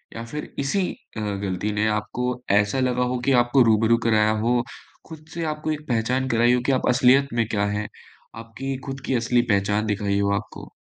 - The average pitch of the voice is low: Yes, low, 120 Hz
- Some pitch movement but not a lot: Yes, average, 3.8 semitones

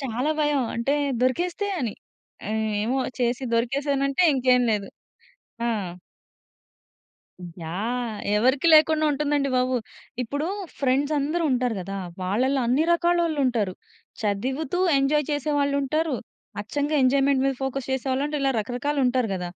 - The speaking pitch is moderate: No, very high, 270 Hz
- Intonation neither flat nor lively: Yes, average, 3.0 semitones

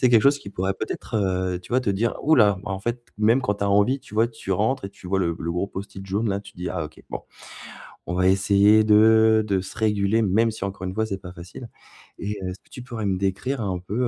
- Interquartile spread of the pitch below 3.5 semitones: Yes, average, 2.8 semitones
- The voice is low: Yes, low, 100 Hz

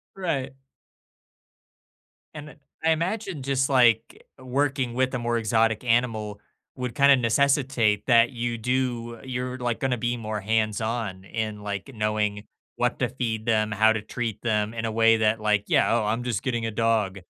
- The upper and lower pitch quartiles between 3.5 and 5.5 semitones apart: No, average, 2.8 semitones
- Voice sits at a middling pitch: No, low, 115 Hz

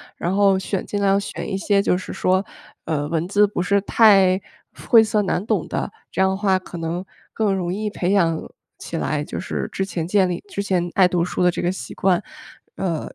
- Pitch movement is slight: Yes, narrow, 2.2 semitones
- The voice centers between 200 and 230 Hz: No, high, 190 Hz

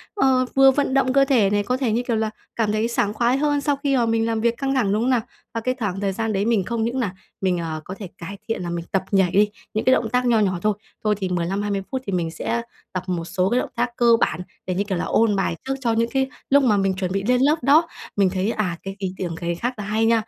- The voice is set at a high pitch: Yes, high, 215 Hz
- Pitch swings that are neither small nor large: Yes, average, 4.5 semitones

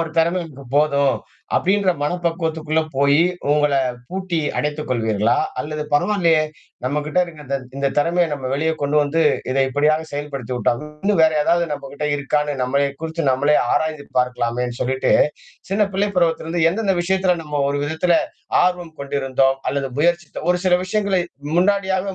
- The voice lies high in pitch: No, medium, 155 Hz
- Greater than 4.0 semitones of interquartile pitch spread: No, average, 3.7 semitones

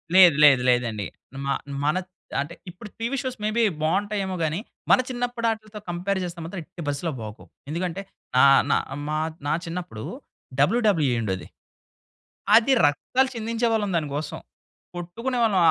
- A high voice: No, medium, 180 Hz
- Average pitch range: No, wide, 6.8 semitones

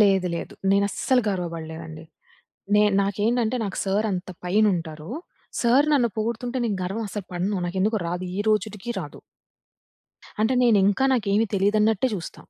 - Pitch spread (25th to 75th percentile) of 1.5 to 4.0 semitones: Yes, average, 3.5 semitones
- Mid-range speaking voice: No, high, 205 Hz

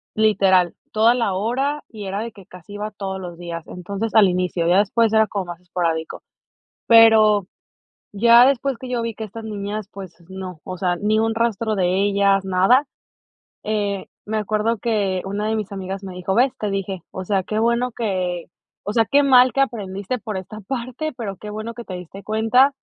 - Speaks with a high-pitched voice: Yes, high, 210 Hz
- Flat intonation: No, average, 3.2 semitones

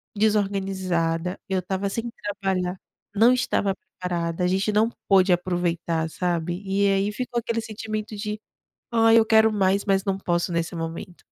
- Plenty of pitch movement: No, average, 3.0 semitones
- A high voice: Yes, high, 195 Hz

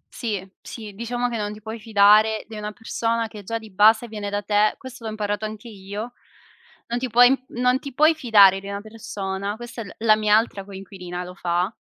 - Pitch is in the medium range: No, high, 215 Hz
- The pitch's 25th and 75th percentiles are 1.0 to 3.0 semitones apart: Yes, narrow, 2.4 semitones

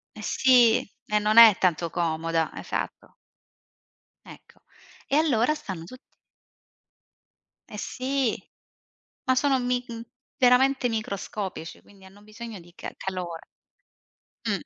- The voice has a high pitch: Yes, high, 215 Hz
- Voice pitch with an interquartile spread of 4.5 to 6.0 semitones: Yes, average, 5.3 semitones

